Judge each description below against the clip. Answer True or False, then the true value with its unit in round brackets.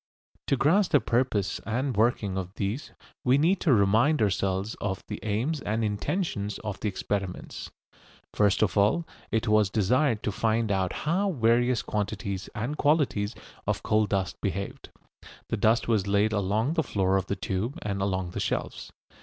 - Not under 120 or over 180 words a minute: True (165 wpm)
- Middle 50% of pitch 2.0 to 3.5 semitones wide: False (4.0 semitones)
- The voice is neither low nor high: False (105 Hz)